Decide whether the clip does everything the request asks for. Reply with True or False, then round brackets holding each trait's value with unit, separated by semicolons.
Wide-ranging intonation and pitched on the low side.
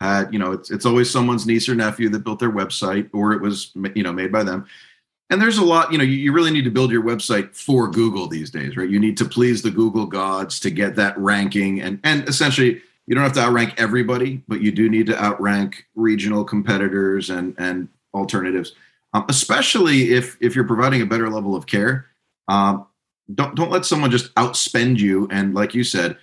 False (3.8 semitones; 110 Hz)